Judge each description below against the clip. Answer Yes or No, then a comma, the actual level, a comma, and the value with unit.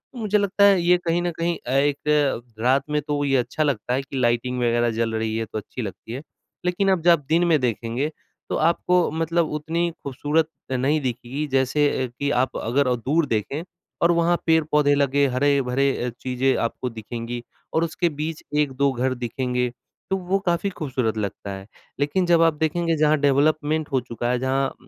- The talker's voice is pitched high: No, medium, 140 Hz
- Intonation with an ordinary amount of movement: Yes, average, 4.6 semitones